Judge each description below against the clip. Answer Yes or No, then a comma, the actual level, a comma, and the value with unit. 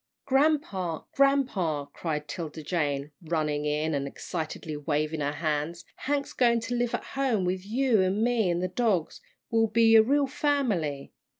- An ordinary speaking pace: Yes, average, 160 wpm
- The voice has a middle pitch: Yes, medium, 180 Hz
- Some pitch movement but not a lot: No, wide, 7.9 semitones